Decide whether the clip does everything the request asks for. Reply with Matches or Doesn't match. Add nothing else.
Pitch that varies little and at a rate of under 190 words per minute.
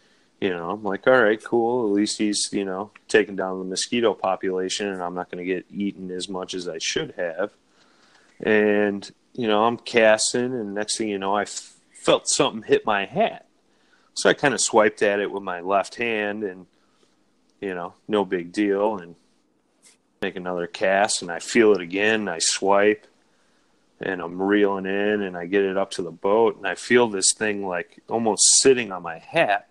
Doesn't match